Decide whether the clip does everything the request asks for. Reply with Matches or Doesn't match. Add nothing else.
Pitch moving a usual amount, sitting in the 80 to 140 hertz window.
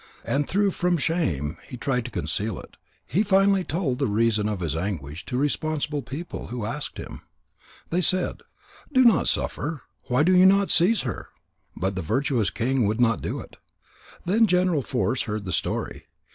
Doesn't match